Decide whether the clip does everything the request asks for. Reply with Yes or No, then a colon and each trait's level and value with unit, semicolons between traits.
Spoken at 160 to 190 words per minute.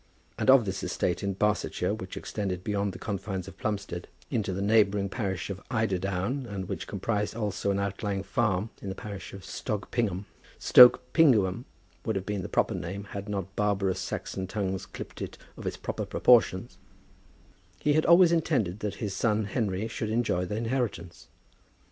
Yes: average, 170 wpm